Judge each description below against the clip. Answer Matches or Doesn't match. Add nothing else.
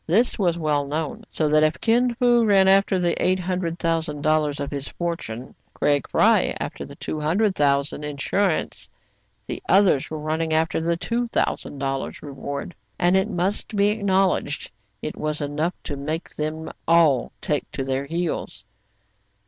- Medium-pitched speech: Matches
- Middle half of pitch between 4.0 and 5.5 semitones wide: Matches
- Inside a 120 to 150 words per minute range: Doesn't match